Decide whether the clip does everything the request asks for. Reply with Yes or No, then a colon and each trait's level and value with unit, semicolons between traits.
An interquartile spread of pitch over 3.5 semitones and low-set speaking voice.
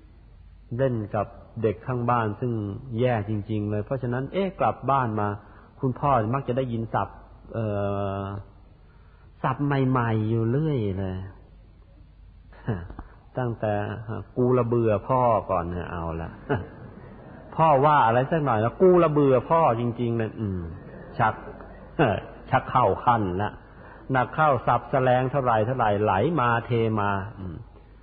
Yes: average, 4.2 semitones; low, 110 Hz